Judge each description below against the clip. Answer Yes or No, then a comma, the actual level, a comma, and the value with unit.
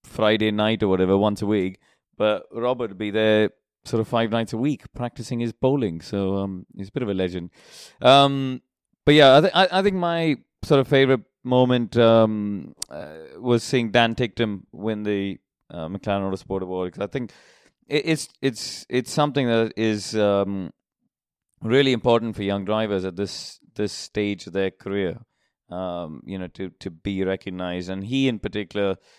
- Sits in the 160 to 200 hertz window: No, low, 110 Hz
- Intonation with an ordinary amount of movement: Yes, average, 4.2 semitones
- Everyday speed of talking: Yes, average, 175 wpm